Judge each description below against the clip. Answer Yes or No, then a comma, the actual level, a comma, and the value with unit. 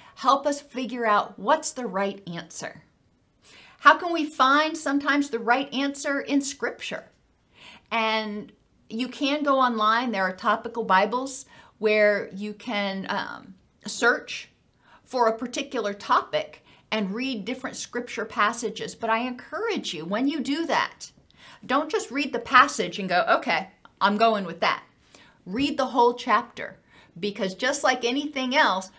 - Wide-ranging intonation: No, average, 4.8 semitones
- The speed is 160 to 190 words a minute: No, average, 145 wpm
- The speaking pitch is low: No, high, 240 Hz